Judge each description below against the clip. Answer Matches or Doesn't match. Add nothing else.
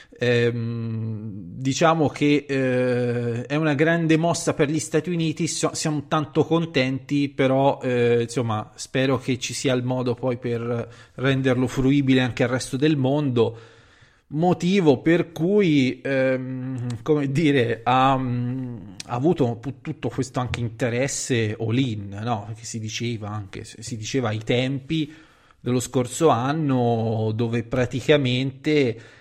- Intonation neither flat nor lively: Matches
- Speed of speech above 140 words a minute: Doesn't match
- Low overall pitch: Matches